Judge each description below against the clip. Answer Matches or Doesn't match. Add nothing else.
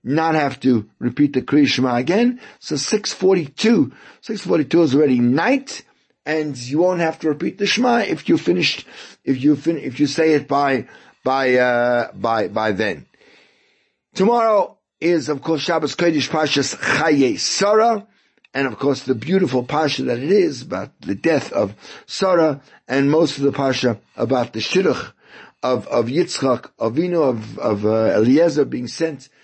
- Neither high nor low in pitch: Matches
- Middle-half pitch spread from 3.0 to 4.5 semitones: Doesn't match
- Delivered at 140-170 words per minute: Matches